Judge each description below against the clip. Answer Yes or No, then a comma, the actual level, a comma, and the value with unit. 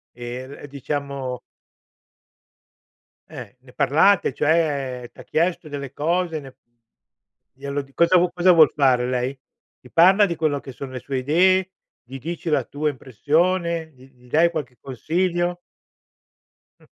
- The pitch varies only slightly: No, average, 4.4 semitones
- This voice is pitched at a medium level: Yes, medium, 145 Hz